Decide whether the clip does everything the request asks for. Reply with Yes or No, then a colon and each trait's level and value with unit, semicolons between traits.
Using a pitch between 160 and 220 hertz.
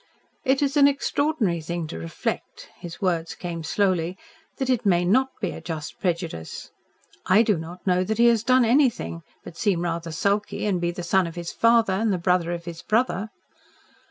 Yes: medium, 185 Hz